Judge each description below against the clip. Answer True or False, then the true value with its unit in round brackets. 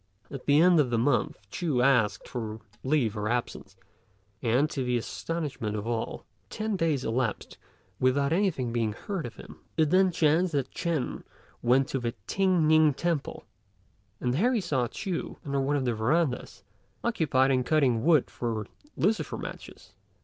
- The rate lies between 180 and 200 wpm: False (165 wpm)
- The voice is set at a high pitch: False (135 Hz)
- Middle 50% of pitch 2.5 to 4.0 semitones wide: False (5.4 semitones)